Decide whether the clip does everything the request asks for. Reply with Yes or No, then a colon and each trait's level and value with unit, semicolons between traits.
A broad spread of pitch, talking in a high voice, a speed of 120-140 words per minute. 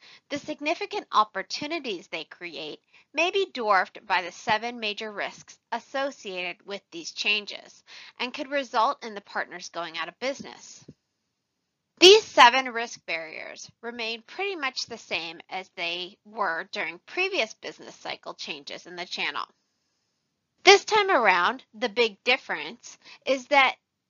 Yes: wide, 6.5 semitones; high, 230 Hz; slow, 135 wpm